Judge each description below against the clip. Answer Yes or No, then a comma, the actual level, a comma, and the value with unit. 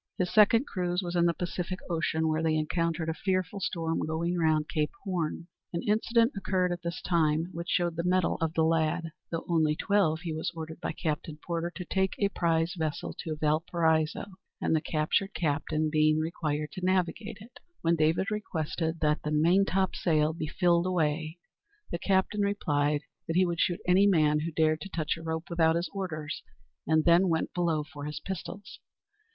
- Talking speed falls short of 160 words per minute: No, average, 180 wpm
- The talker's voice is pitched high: No, medium, 165 Hz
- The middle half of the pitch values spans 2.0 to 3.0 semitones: Yes, narrow, 2.5 semitones